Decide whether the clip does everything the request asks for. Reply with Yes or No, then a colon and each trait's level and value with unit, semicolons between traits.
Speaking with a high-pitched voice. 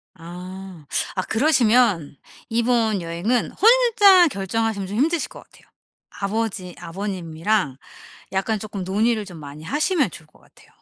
Yes: high, 205 Hz